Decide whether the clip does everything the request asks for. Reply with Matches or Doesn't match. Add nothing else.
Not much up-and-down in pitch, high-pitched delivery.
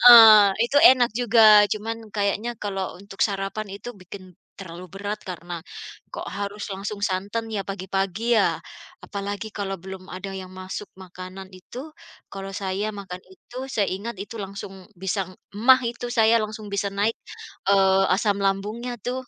Matches